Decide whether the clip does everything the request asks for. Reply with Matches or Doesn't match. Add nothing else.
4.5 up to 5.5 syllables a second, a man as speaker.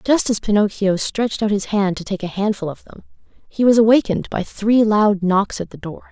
Doesn't match